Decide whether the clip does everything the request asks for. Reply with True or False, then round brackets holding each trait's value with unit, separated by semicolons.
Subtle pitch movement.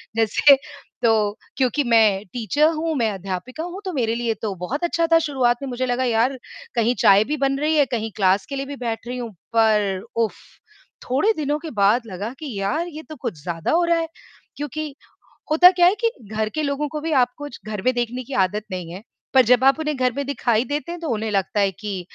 False (5.5 semitones)